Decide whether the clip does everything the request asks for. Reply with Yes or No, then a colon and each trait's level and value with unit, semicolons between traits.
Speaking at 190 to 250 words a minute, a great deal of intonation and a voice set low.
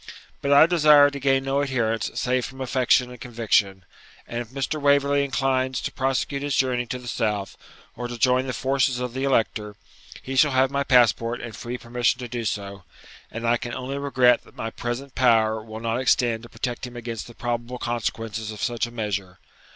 No: average, 200 wpm; narrow, 2.5 semitones; low, 125 Hz